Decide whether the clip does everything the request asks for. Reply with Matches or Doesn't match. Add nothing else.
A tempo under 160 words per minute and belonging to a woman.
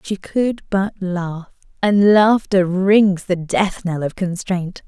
Matches